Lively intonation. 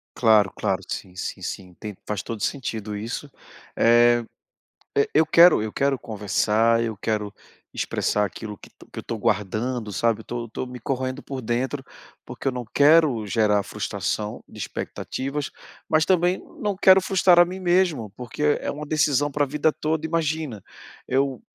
Yes: wide, 5.8 semitones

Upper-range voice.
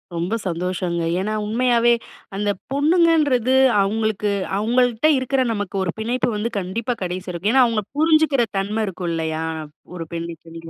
Yes: high, 215 Hz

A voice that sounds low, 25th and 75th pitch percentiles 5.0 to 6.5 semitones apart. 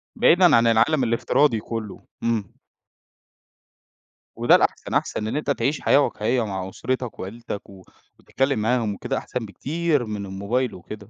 No: low, 115 Hz; average, 3.9 semitones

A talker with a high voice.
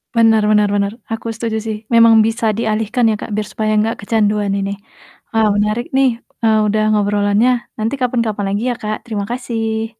Yes: high, 220 Hz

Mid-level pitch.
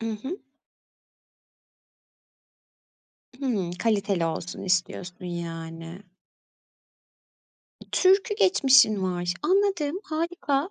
No: high, 215 Hz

